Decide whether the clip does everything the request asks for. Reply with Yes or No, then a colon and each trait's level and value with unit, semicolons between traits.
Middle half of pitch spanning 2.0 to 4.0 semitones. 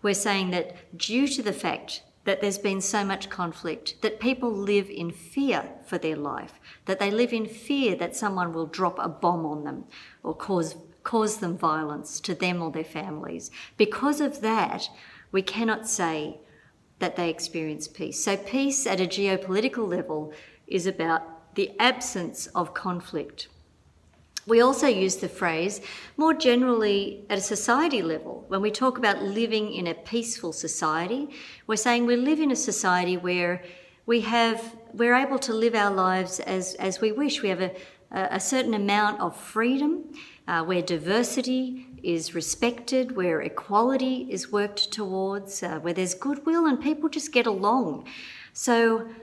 No: average, 5.1 semitones